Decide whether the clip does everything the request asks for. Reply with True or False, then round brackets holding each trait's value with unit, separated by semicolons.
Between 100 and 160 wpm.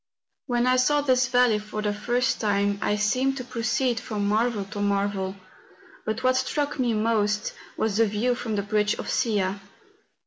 False (175 wpm)